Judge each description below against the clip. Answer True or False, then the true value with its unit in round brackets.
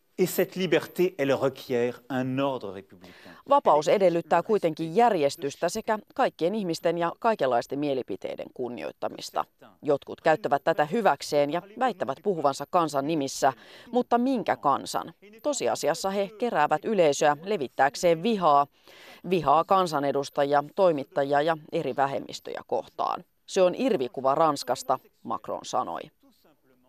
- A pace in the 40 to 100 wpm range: True (95 wpm)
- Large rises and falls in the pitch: True (6.3 semitones)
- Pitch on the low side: False (165 Hz)